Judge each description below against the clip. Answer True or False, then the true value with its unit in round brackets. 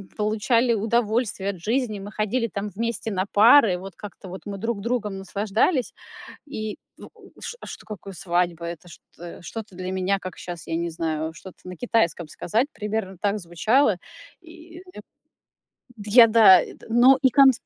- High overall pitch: True (210 Hz)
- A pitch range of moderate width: True (4.0 semitones)